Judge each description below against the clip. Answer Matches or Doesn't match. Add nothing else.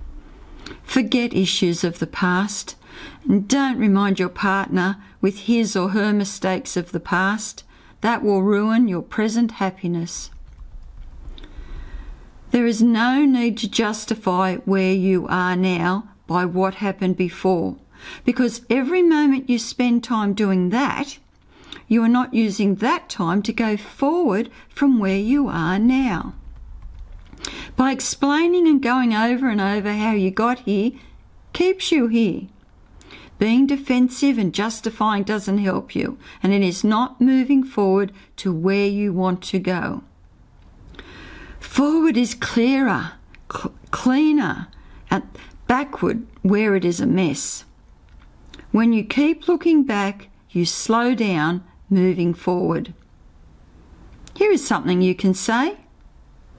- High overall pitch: Matches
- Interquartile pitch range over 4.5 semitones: Matches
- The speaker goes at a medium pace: Doesn't match